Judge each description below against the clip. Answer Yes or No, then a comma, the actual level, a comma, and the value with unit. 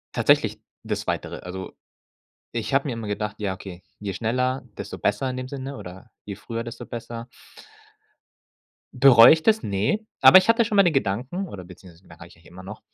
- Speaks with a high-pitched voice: No, low, 115 Hz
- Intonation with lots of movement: Yes, wide, 5.8 semitones